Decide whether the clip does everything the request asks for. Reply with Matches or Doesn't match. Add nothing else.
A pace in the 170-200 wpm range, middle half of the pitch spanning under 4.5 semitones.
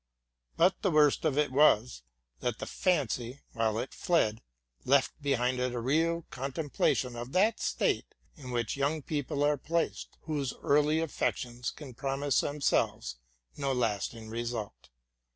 Doesn't match